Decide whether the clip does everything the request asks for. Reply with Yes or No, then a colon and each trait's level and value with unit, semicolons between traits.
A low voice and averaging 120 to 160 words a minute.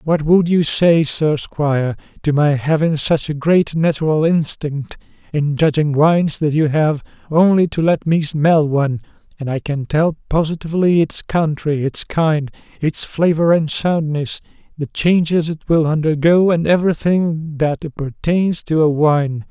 No: medium, 155 Hz; average, 155 wpm